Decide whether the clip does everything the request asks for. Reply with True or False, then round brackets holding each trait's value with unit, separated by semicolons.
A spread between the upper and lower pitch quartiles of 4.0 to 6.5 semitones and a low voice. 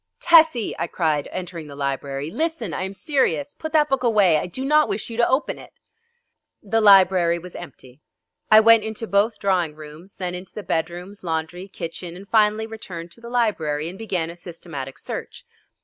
False (5.2 semitones; 190 Hz)